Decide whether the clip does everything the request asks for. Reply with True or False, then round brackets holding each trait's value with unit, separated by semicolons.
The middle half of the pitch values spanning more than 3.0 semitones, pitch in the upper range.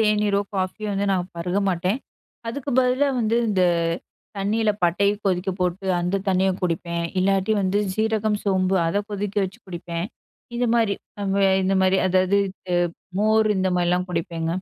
False (2.5 semitones; 195 Hz)